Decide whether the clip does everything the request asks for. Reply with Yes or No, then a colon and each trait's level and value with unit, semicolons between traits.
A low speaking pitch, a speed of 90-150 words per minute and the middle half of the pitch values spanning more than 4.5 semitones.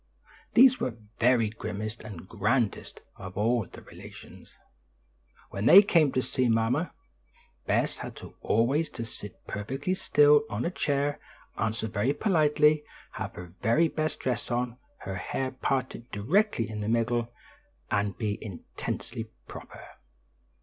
Yes: low, 120 Hz; slow, 135 wpm; average, 5.2 semitones